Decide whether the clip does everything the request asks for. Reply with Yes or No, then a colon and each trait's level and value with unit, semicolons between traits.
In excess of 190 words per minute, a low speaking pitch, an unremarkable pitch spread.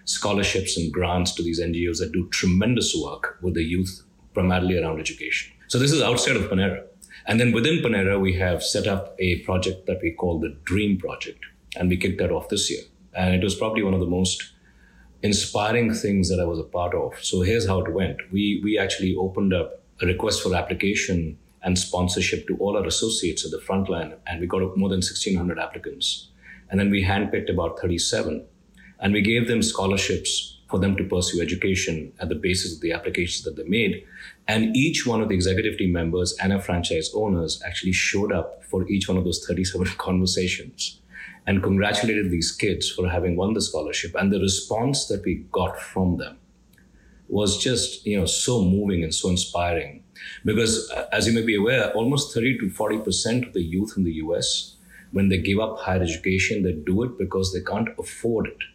No: average, 200 wpm; very low, 95 Hz; narrow, 2.0 semitones